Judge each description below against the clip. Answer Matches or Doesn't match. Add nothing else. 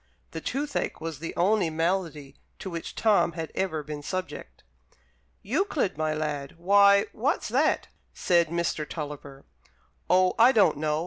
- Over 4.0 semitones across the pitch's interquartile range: Matches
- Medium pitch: Matches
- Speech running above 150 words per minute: Doesn't match